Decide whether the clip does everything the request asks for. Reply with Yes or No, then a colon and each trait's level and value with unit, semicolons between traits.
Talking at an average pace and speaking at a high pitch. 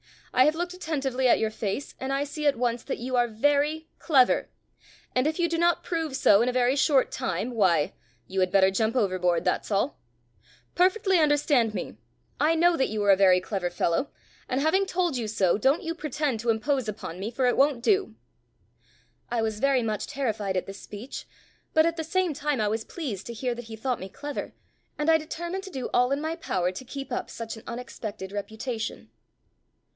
No: fast, 210 wpm; very high, 255 Hz